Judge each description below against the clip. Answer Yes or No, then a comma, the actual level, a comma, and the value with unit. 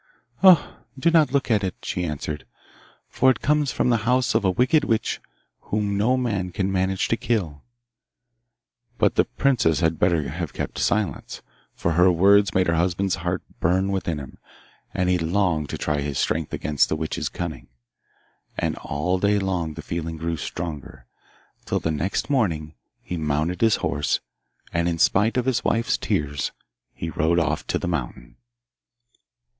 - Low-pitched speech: Yes, very low, 90 Hz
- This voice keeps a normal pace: Yes, average, 170 wpm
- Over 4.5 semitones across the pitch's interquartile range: Yes, average, 5.0 semitones